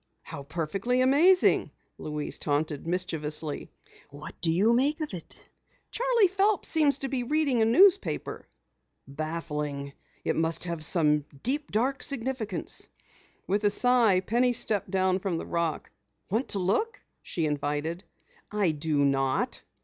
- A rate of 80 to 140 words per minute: Yes, slow, 135 wpm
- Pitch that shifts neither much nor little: No, wide, 8.8 semitones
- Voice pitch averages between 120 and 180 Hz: No, high, 190 Hz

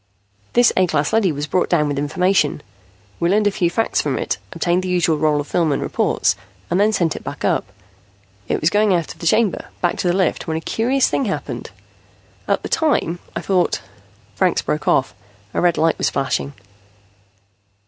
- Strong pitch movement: No, average, 4.2 semitones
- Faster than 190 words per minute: Yes, average, 200 wpm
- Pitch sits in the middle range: Yes, medium, 175 Hz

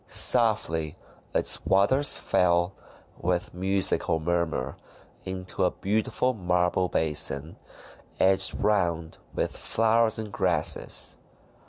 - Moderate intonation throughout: Yes, average, 3.6 semitones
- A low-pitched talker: Yes, very low, 90 Hz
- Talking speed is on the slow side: Yes, slow, 90 wpm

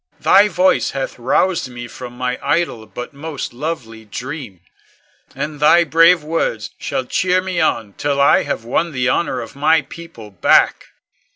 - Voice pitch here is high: No, medium, 140 Hz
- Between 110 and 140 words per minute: No, average, 160 wpm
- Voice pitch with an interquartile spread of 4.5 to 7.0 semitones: Yes, average, 5.3 semitones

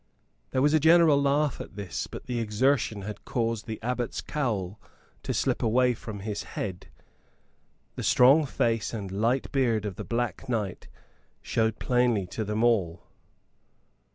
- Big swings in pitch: No, average, 3.5 semitones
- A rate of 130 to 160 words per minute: Yes, average, 155 wpm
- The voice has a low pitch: Yes, low, 115 Hz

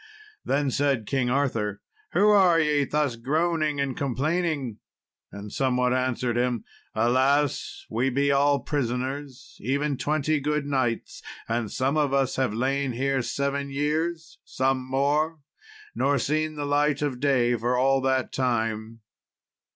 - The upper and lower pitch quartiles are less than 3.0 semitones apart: Yes, narrow, 2.6 semitones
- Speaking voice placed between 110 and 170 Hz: Yes, low, 135 Hz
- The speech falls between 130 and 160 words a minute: Yes, average, 140 wpm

